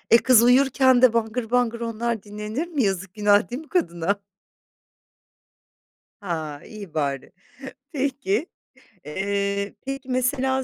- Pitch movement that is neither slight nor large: Yes, average, 4.5 semitones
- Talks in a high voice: Yes, high, 230 Hz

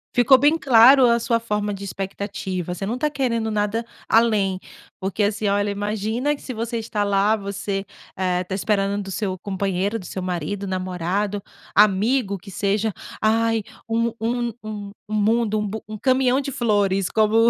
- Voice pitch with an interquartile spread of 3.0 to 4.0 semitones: No, narrow, 2.6 semitones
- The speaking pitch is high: Yes, high, 210 Hz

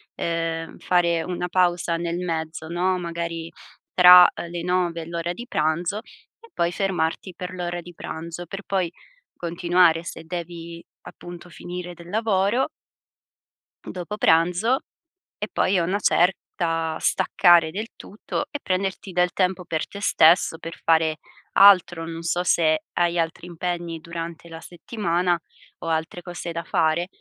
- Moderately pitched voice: Yes, medium, 175 Hz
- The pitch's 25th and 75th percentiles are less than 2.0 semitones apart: Yes, narrow, 1.5 semitones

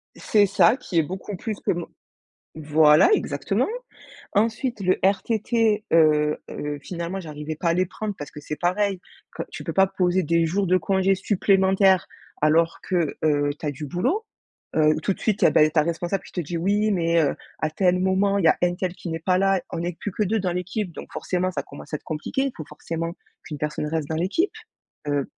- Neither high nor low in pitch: Yes, medium, 180 Hz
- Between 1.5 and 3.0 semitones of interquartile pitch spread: No, average, 3.7 semitones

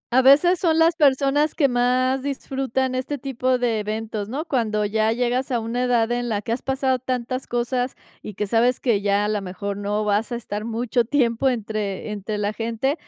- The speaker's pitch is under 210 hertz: No, high, 240 Hz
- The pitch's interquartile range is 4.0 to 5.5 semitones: No, average, 3.5 semitones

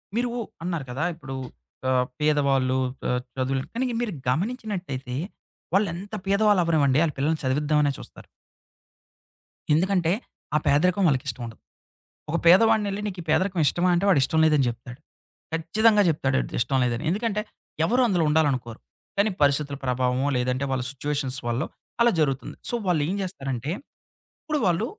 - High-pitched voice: No, medium, 150 Hz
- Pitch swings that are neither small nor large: No, wide, 6.3 semitones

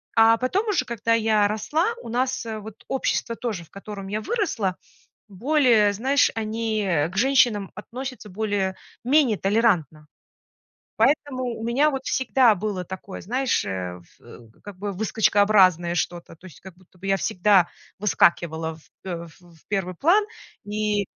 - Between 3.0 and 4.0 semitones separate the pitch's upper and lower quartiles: No, average, 4.5 semitones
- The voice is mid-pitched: No, high, 210 Hz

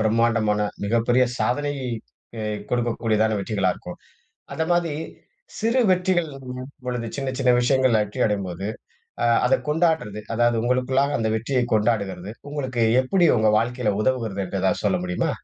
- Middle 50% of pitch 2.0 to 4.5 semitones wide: Yes, average, 3.7 semitones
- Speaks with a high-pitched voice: No, low, 120 Hz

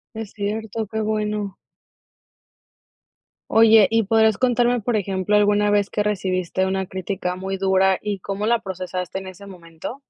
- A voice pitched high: Yes, high, 205 Hz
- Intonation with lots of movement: No, narrow, 2.4 semitones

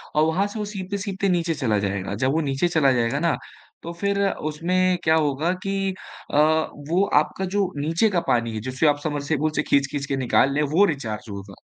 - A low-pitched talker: No, medium, 155 Hz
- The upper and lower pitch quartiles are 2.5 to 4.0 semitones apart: No, average, 5.2 semitones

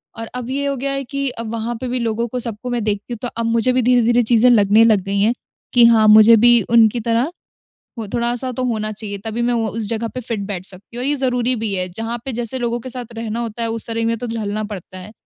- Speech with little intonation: Yes, narrow, 2.0 semitones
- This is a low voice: No, high, 230 Hz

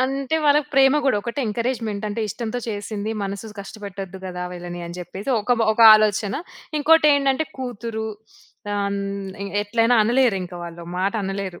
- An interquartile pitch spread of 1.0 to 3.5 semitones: No, average, 4.1 semitones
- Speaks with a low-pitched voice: No, high, 215 Hz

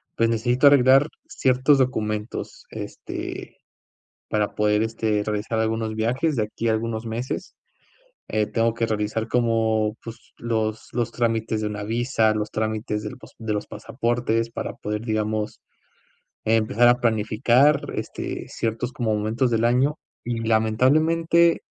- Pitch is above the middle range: No, low, 115 Hz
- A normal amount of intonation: No, narrow, 2.0 semitones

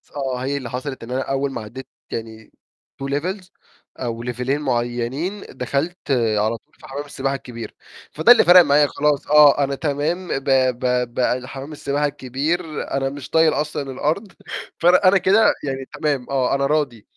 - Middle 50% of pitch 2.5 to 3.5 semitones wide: Yes, average, 3.0 semitones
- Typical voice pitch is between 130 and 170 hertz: Yes, medium, 140 Hz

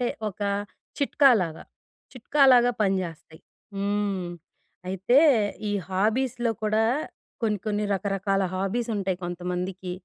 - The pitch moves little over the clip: No, average, 3.7 semitones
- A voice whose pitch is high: Yes, high, 200 Hz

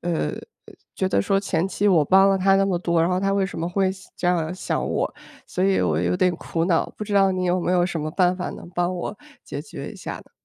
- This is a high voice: No, medium, 180 Hz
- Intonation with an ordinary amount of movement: No, narrow, 2.1 semitones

